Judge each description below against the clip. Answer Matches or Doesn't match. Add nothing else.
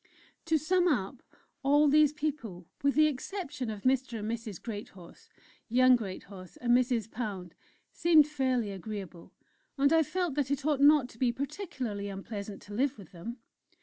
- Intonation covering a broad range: Matches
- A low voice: Doesn't match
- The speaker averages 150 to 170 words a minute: Matches